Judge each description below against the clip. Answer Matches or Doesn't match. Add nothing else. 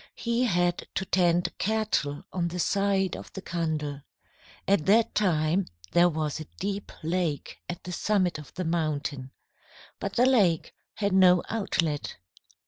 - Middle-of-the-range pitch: Matches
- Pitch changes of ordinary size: Matches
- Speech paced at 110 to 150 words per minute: Matches